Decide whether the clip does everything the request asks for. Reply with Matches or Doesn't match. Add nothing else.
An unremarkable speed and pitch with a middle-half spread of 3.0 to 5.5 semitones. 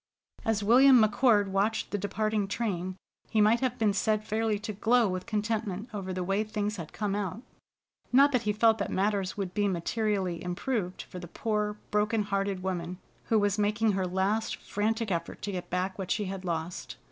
Doesn't match